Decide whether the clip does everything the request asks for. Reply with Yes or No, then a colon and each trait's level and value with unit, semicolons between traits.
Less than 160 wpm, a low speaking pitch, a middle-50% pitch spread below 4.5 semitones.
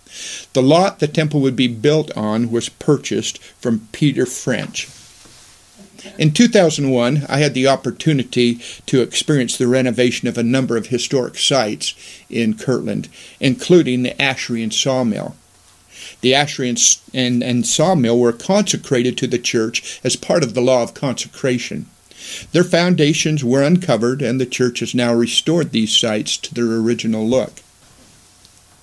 Yes: average, 145 wpm; low, 125 Hz; average, 3.8 semitones